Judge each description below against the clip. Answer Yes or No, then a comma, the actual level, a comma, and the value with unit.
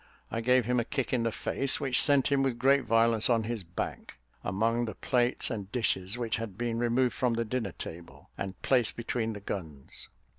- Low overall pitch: Yes, low, 115 Hz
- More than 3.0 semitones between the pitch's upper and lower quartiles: No, average, 2.7 semitones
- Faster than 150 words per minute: Yes, average, 200 wpm